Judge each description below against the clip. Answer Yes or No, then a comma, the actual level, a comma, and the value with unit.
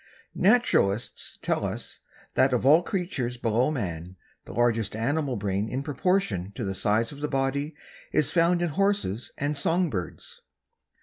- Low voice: Yes, low, 130 Hz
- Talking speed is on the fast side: No, average, 150 wpm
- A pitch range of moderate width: No, wide, 6.7 semitones